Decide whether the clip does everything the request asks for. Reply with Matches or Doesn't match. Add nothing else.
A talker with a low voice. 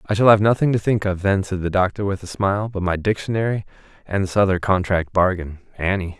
Matches